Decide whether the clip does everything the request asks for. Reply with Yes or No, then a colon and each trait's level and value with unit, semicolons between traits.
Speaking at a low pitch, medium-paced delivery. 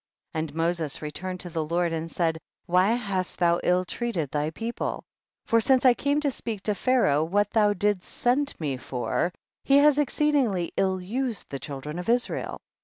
No: medium, 185 Hz; average, 185 wpm